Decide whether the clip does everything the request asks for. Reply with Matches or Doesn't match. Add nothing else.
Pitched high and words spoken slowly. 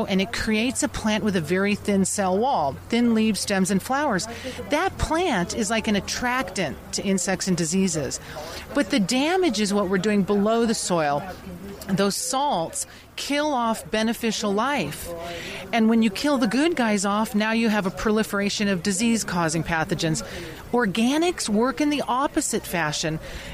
Doesn't match